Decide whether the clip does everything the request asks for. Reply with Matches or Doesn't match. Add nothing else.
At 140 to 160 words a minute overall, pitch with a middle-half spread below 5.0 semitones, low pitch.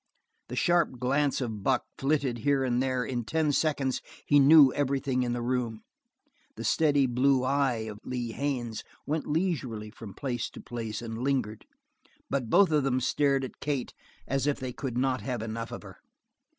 Doesn't match